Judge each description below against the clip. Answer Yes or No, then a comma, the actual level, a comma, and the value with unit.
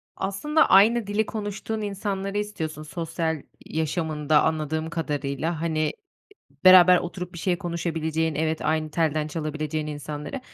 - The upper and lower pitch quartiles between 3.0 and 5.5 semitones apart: Yes, average, 3.8 semitones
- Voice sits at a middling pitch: Yes, medium, 160 Hz